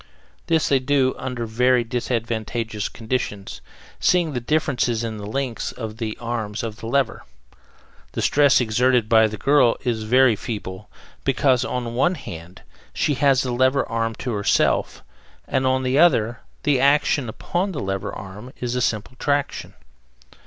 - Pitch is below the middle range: Yes, low, 120 Hz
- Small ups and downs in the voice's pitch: No, average, 3.2 semitones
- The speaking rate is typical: Yes, average, 160 wpm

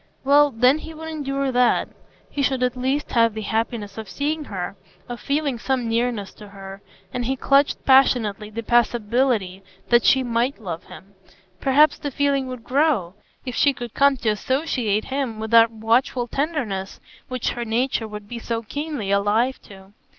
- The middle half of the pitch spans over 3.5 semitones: Yes, average, 3.9 semitones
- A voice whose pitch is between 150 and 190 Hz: No, high, 240 Hz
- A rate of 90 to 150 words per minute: No, average, 170 wpm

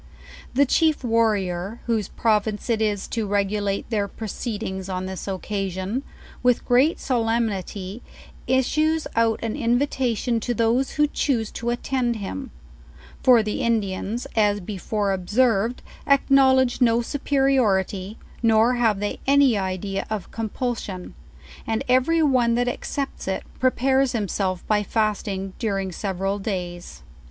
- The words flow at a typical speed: No, slow, 125 wpm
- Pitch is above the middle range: Yes, high, 225 Hz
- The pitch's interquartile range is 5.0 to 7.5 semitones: No, average, 4.0 semitones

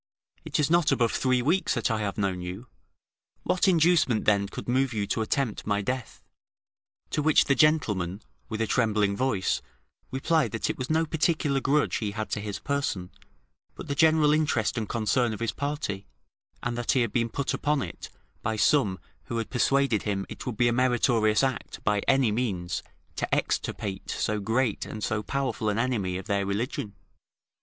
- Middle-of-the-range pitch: No, low, 115 Hz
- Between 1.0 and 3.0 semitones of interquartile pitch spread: No, average, 4.9 semitones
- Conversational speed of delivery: Yes, average, 185 wpm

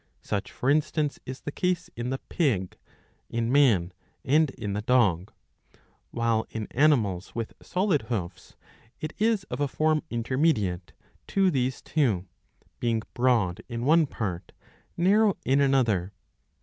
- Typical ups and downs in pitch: No, wide, 6.2 semitones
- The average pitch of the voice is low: Yes, low, 125 Hz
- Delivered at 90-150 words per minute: Yes, average, 140 wpm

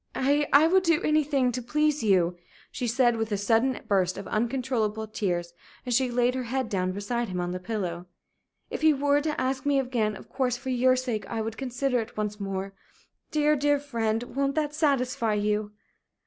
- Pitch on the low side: No, high, 245 Hz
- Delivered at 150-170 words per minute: No, average, 195 wpm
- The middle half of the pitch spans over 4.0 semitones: Yes, average, 4.5 semitones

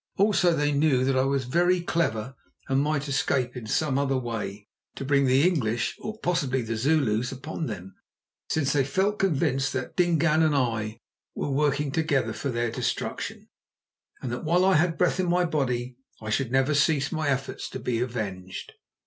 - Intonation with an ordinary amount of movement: Yes, average, 4.5 semitones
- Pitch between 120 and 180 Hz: Yes, low, 135 Hz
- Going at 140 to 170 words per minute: No, average, 180 wpm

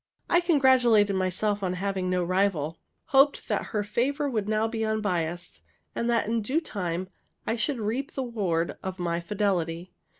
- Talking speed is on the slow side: No, average, 165 wpm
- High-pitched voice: Yes, high, 205 Hz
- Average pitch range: Yes, average, 4.4 semitones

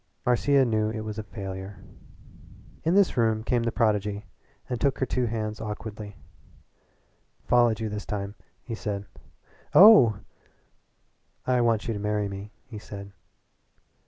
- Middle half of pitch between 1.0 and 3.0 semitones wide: Yes, narrow, 2.4 semitones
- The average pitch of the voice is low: Yes, low, 110 Hz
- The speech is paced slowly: No, average, 145 wpm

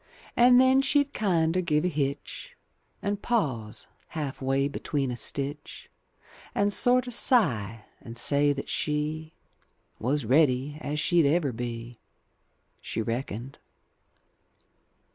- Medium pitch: Yes, medium, 145 Hz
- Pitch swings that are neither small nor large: No, wide, 6.0 semitones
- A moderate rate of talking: No, slow, 115 wpm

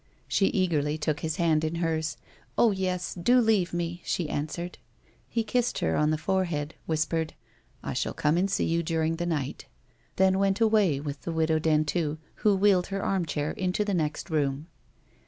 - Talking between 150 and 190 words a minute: Yes, average, 185 wpm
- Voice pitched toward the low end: No, medium, 170 Hz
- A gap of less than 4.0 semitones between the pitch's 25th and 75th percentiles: Yes, average, 3.5 semitones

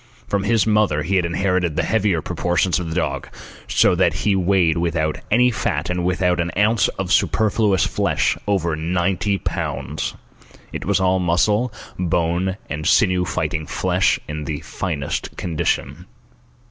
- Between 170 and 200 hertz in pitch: No, very low, 90 Hz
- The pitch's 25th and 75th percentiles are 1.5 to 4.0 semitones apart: Yes, average, 2.9 semitones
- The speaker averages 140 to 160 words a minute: Yes, average, 150 wpm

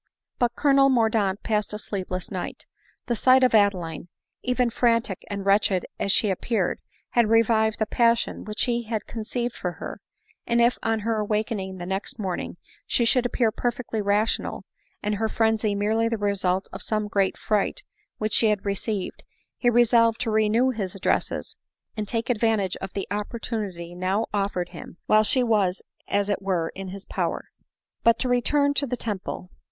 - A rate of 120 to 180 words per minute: Yes, average, 175 wpm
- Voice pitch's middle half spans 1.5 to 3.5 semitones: Yes, average, 2.9 semitones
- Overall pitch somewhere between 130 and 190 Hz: No, high, 215 Hz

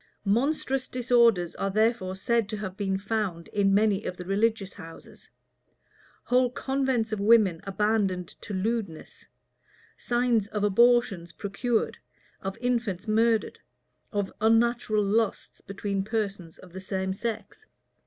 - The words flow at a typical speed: No, slow, 125 wpm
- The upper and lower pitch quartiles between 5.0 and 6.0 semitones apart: No, average, 3.3 semitones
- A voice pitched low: No, high, 210 Hz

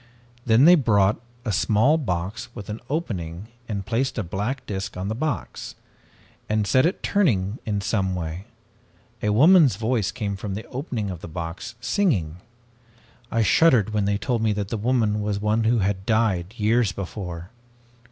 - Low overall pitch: Yes, low, 105 Hz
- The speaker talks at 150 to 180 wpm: Yes, average, 170 wpm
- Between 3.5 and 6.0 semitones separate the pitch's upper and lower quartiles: Yes, average, 3.9 semitones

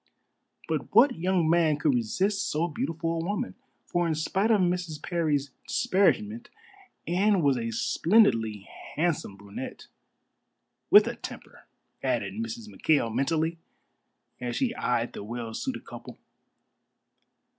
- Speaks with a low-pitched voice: No, medium, 165 Hz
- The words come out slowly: Yes, slow, 125 wpm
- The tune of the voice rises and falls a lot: Yes, wide, 6.4 semitones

